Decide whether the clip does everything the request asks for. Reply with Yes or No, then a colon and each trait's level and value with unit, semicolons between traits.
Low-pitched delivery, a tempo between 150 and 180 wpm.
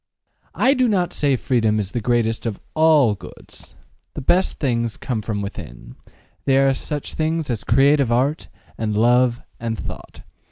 Yes: low, 125 Hz; average, 160 wpm